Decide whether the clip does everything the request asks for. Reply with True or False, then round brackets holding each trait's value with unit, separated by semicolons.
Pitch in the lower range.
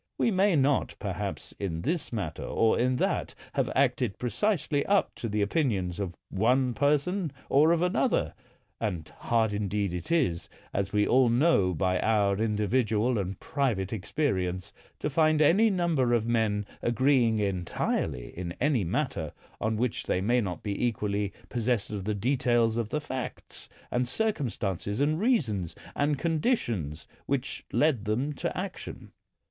True (115 Hz)